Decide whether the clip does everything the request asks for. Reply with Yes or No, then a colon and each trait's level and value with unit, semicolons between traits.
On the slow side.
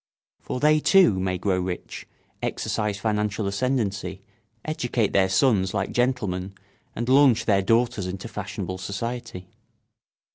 Yes: slow, 120 wpm